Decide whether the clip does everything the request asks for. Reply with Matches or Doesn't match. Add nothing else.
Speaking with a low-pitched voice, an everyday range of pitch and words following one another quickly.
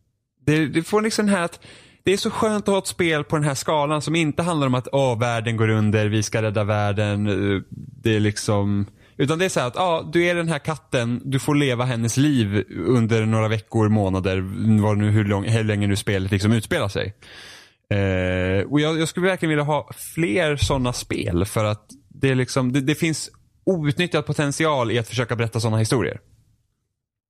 Doesn't match